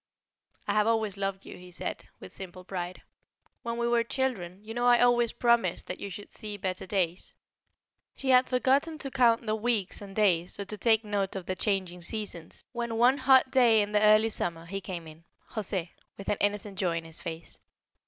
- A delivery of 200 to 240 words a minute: Yes, fast, 205 wpm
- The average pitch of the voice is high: Yes, high, 205 Hz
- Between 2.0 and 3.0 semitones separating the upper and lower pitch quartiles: No, average, 4.3 semitones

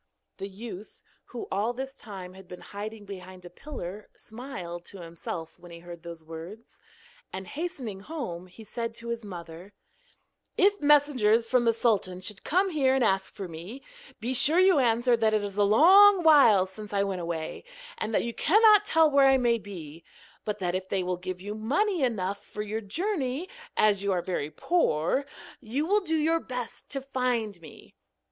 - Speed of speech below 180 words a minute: No, average, 185 wpm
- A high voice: Yes, high, 215 Hz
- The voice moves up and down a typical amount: No, wide, 6.5 semitones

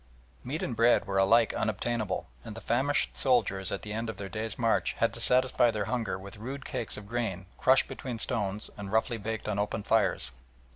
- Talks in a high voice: No, low, 110 Hz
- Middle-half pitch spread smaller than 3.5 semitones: Yes, average, 2.8 semitones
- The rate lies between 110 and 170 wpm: No, average, 200 wpm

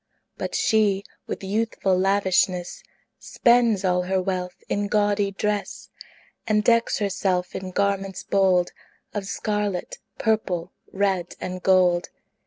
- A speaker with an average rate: No, slow, 115 wpm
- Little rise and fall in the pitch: Yes, narrow, 2.1 semitones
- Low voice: No, high, 195 Hz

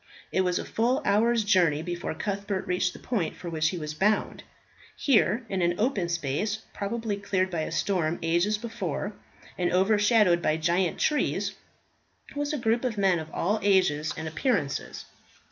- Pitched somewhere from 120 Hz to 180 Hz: No, high, 190 Hz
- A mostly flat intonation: No, average, 3.9 semitones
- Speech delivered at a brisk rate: No, average, 165 wpm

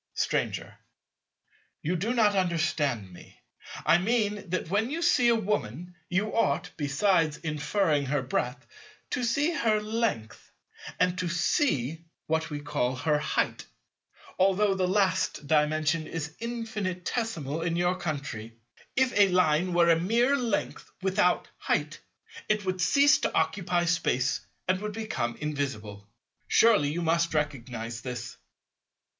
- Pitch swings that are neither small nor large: No, wide, 5.9 semitones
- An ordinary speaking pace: No, slow, 125 wpm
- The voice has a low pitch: No, medium, 175 Hz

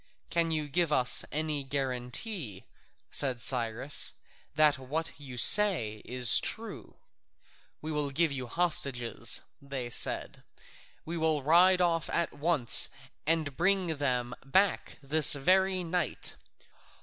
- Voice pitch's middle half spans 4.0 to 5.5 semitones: Yes, average, 4.7 semitones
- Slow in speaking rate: Yes, slow, 120 wpm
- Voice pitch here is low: No, medium, 150 Hz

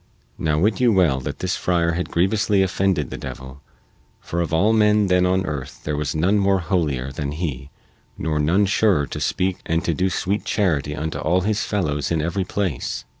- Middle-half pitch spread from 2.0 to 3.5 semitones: No, average, 4.4 semitones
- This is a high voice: No, very low, 85 Hz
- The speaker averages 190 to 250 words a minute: Yes, average, 195 wpm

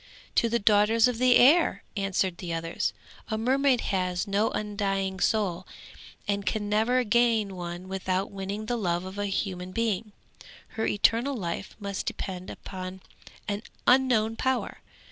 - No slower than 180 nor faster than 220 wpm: No, average, 145 wpm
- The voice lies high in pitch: Yes, high, 205 Hz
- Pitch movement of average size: Yes, average, 3.3 semitones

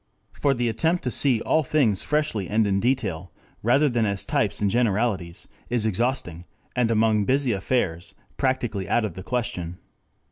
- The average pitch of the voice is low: Yes, low, 115 Hz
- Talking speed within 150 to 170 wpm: Yes, average, 165 wpm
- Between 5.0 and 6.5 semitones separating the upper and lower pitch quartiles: No, average, 4.5 semitones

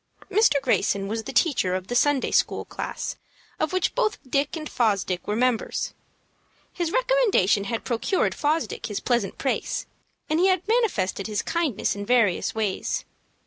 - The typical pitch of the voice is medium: No, very high, 255 Hz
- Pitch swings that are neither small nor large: No, wide, 8.5 semitones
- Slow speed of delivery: No, average, 155 wpm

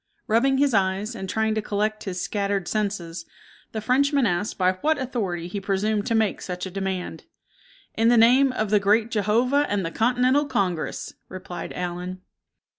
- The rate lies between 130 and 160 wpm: No, average, 170 wpm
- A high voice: Yes, high, 210 Hz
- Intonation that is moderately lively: Yes, average, 3.8 semitones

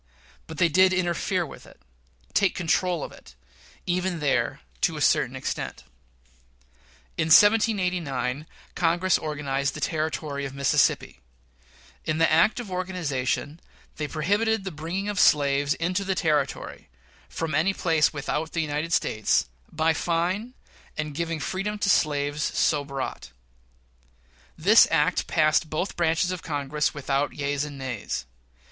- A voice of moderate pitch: Yes, medium, 160 Hz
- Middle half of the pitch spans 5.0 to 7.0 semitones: No, average, 4.0 semitones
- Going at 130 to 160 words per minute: Yes, slow, 135 wpm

